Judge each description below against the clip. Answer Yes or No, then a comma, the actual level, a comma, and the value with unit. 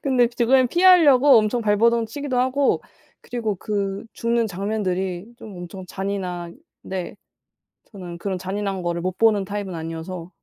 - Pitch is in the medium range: No, high, 205 Hz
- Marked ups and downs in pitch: No, average, 4.3 semitones